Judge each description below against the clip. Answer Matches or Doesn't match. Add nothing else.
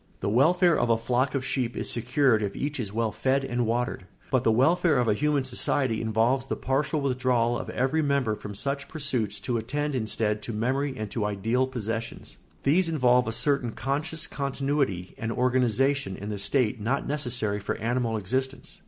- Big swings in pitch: Doesn't match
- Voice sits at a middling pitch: Doesn't match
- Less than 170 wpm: Doesn't match